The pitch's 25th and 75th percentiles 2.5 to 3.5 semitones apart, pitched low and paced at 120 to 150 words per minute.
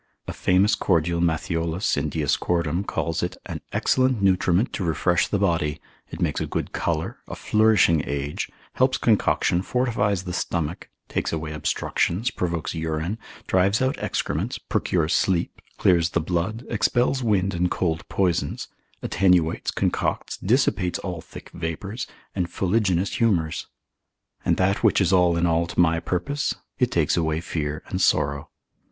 Yes: average, 3.2 semitones; very low, 90 Hz; average, 145 wpm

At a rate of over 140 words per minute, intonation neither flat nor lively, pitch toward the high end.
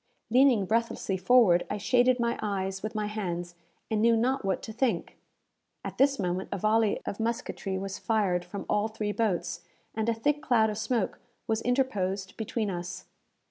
Yes: average, 175 wpm; average, 3.5 semitones; high, 215 Hz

